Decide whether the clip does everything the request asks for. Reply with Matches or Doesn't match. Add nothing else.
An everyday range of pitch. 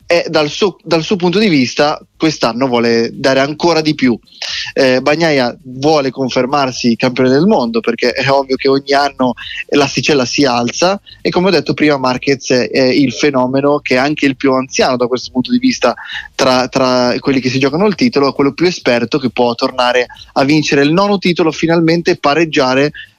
Matches